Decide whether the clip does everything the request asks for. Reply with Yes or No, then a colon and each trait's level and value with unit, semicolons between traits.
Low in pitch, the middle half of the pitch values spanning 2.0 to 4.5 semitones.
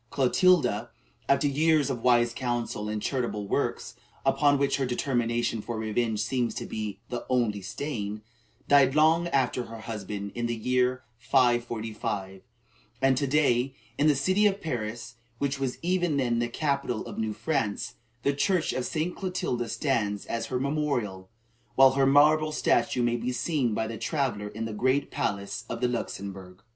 Yes: low, 125 Hz; average, 4.0 semitones